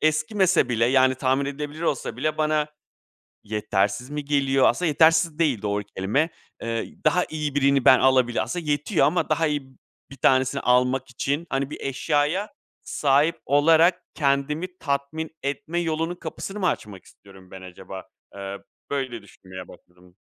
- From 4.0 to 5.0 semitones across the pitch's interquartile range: Yes, average, 4.4 semitones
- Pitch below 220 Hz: Yes, medium, 140 Hz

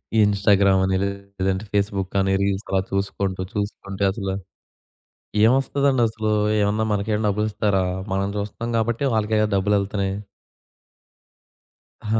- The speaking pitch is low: Yes, low, 100 Hz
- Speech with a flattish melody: Yes, narrow, 1.8 semitones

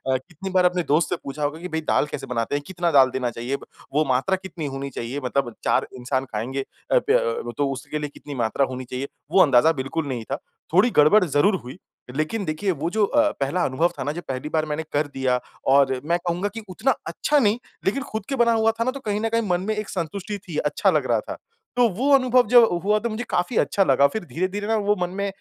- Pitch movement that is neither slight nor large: No, wide, 7.2 semitones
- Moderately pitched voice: Yes, medium, 170 Hz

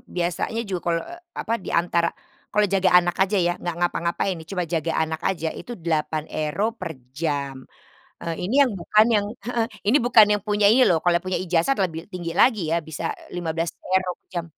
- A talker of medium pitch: Yes, medium, 175 Hz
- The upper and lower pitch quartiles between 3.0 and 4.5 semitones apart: Yes, average, 3.4 semitones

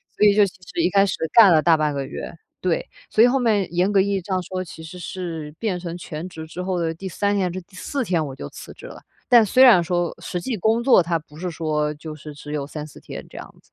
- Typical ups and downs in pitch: Yes, average, 3.7 semitones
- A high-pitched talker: No, medium, 180 Hz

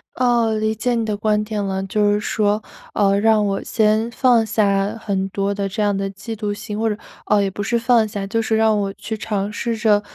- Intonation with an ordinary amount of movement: No, narrow, 1.7 semitones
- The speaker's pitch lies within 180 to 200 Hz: No, high, 210 Hz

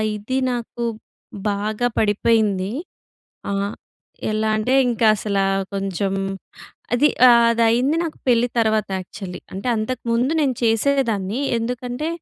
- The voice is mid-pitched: No, high, 225 Hz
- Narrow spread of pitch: No, average, 3.1 semitones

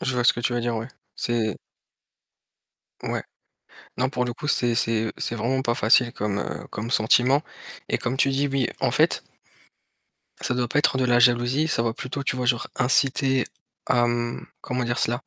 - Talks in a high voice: No, low, 120 Hz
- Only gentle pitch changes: Yes, narrow, 1.9 semitones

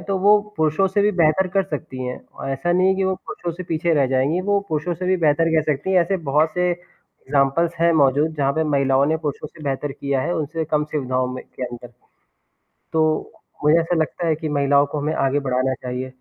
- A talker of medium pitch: Yes, medium, 155 Hz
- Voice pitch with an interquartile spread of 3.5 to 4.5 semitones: Yes, average, 3.9 semitones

